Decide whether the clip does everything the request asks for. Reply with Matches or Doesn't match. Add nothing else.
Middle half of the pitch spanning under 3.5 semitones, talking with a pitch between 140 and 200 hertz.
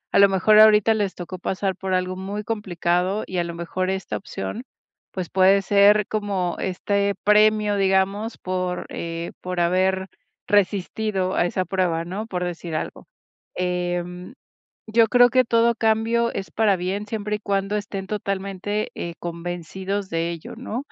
Matches